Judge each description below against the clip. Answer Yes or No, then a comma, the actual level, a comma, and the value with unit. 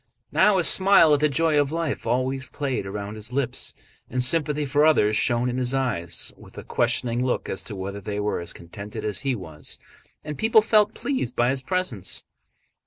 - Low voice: Yes, low, 125 Hz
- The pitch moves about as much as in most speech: No, wide, 6.2 semitones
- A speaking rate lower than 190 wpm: No, average, 195 wpm